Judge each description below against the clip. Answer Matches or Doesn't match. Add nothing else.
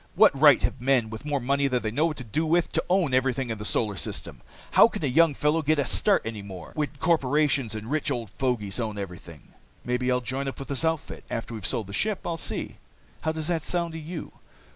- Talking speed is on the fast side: Matches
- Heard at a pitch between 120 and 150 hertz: Matches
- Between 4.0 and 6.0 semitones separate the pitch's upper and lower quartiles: Matches